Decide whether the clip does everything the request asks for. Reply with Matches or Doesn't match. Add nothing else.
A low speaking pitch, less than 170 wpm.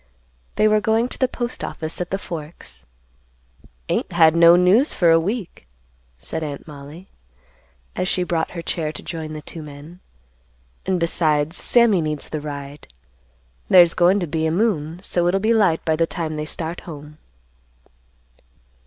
Doesn't match